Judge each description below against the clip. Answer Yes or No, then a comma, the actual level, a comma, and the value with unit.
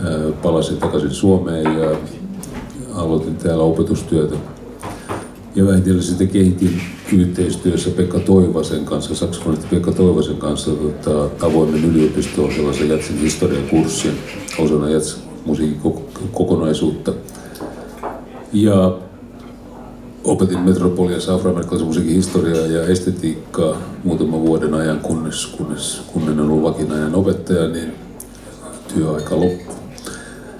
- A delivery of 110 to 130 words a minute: No, average, 100 wpm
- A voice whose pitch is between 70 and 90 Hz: Yes, very low, 80 Hz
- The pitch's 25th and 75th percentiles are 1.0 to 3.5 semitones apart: Yes, average, 2.8 semitones